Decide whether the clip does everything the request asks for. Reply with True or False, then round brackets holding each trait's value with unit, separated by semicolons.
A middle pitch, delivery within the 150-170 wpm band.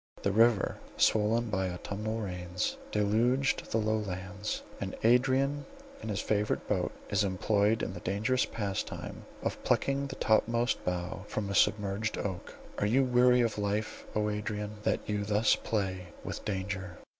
False (105 Hz; 155 wpm)